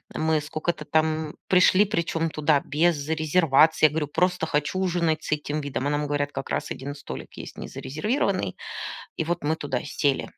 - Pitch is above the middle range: No, medium, 155 Hz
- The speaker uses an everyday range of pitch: No, narrow, 2.2 semitones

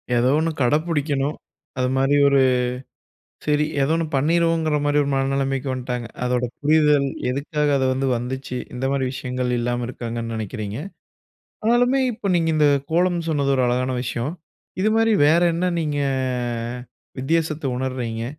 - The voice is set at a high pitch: No, medium, 140 Hz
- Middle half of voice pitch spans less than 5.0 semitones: Yes, average, 3.9 semitones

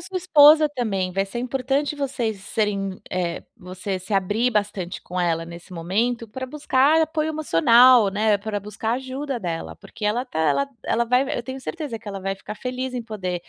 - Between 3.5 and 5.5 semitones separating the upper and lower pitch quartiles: Yes, average, 5.1 semitones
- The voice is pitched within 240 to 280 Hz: No, high, 225 Hz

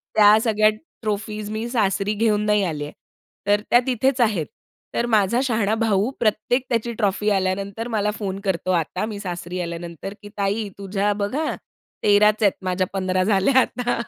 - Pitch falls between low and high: No, high, 205 Hz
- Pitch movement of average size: No, narrow, 2.2 semitones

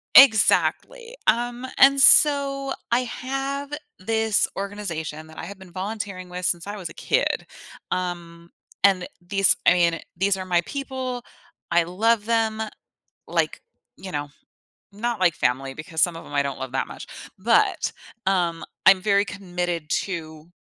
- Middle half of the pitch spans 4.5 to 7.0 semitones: Yes, average, 5.2 semitones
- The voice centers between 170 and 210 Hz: Yes, high, 190 Hz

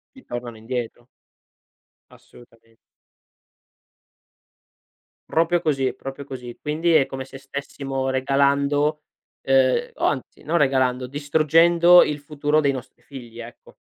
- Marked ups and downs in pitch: No, average, 2.7 semitones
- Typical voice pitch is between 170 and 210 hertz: No, low, 135 Hz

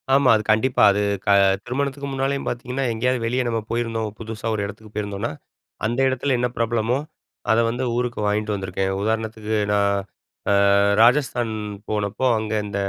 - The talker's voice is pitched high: No, low, 115 Hz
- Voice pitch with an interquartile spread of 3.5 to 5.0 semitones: No, average, 2.9 semitones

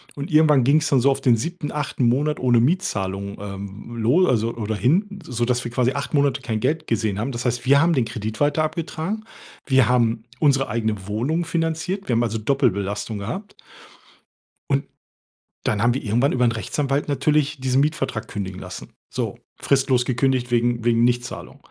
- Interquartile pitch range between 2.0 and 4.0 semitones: No, average, 4.5 semitones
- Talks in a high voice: No, low, 125 Hz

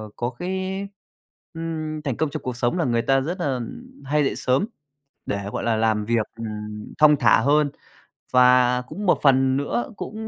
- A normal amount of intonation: Yes, average, 4.7 semitones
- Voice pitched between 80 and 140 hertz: Yes, low, 135 Hz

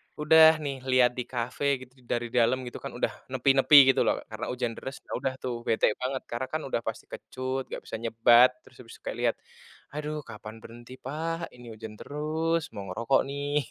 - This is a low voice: Yes, low, 130 Hz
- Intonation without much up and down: No, average, 3.2 semitones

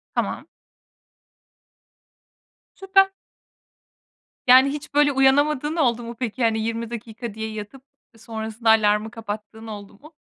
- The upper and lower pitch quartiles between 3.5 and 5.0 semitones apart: Yes, average, 3.8 semitones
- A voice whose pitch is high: Yes, high, 230 Hz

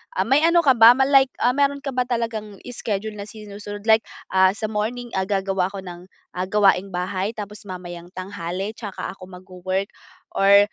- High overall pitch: Yes, high, 205 Hz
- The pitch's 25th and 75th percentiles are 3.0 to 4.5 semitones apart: Yes, average, 3.3 semitones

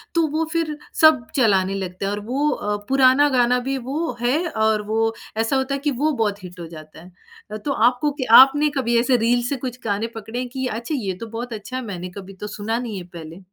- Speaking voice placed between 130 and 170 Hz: No, high, 235 Hz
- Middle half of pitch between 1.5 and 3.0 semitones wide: No, average, 4.6 semitones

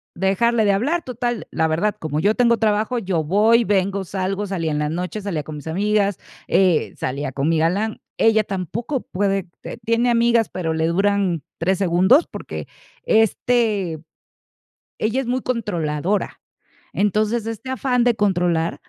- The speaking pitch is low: No, high, 200 Hz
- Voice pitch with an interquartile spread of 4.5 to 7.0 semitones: Yes, average, 4.8 semitones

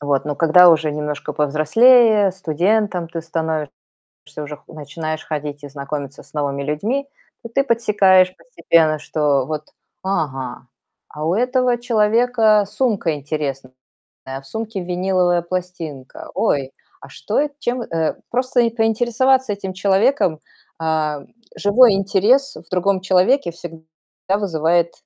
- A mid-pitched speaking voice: Yes, medium, 175 Hz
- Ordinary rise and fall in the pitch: No, wide, 6.3 semitones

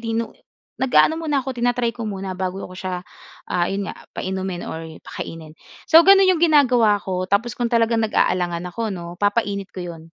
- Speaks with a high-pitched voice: Yes, high, 205 Hz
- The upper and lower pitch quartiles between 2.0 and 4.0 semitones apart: No, average, 4.7 semitones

